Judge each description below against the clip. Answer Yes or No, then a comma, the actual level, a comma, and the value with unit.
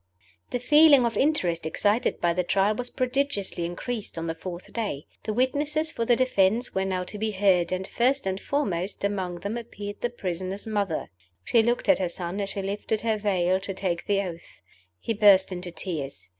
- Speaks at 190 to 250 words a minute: Yes, average, 195 wpm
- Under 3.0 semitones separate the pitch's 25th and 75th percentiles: No, average, 4.6 semitones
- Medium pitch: No, high, 200 Hz